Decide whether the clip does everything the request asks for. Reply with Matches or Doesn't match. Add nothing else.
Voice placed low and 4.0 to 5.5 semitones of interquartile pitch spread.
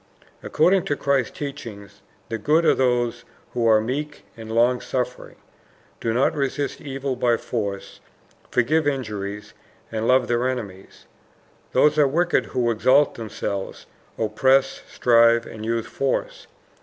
Doesn't match